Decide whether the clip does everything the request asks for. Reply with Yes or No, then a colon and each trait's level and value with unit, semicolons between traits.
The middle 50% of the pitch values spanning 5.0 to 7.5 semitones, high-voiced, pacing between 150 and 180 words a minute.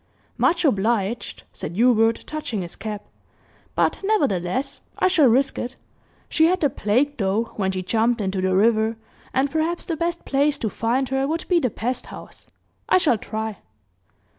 Yes: wide, 5.5 semitones; high, 240 Hz; average, 165 wpm